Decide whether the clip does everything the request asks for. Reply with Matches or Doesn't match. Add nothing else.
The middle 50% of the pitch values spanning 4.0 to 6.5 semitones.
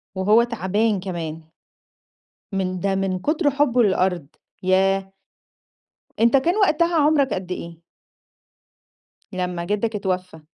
Matches